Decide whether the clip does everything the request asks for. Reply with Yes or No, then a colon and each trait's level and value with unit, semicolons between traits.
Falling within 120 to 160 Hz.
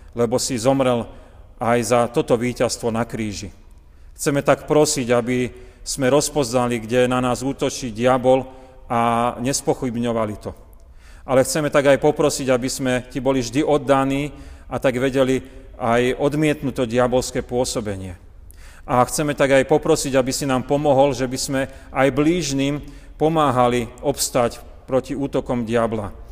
Yes: low, 130 Hz